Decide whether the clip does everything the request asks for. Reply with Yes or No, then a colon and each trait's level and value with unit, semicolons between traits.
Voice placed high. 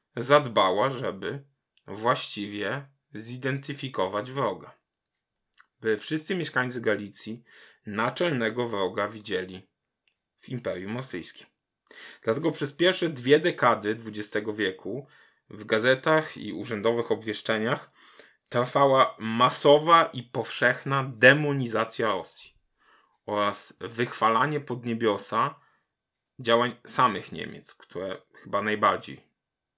No: low, 125 Hz